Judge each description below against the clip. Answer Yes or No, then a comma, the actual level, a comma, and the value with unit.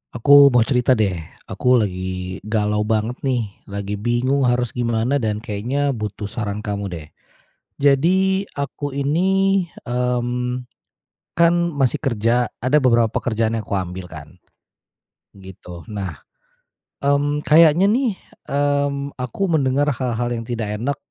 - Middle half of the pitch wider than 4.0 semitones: Yes, average, 5.1 semitones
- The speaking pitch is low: Yes, low, 120 Hz